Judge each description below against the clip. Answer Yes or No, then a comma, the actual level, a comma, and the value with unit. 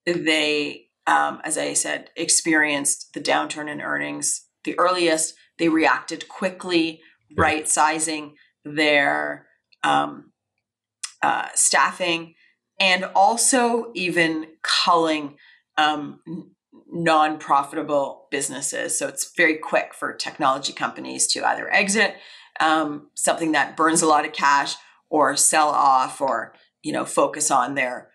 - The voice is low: No, medium, 160 Hz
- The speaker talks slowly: Yes, slow, 115 wpm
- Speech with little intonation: Yes, narrow, 2.2 semitones